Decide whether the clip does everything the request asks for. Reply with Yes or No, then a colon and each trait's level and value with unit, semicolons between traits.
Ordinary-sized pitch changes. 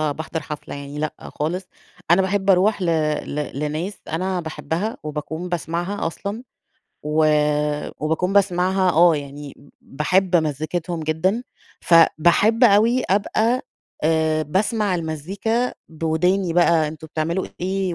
Yes: average, 3.6 semitones